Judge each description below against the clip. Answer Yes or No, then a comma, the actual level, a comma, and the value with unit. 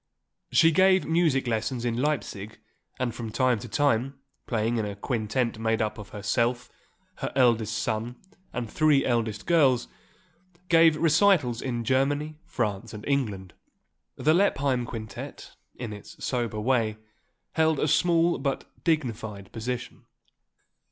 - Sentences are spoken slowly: Yes, slow, 130 wpm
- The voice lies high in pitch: No, low, 125 Hz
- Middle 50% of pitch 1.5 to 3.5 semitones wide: No, average, 4.7 semitones